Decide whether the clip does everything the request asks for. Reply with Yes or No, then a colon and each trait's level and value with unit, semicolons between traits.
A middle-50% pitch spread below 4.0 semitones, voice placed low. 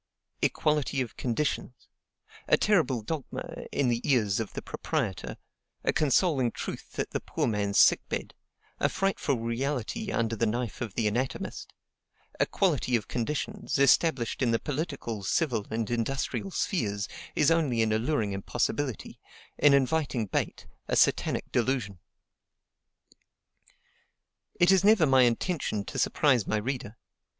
No: average, 4.8 semitones; low, 125 Hz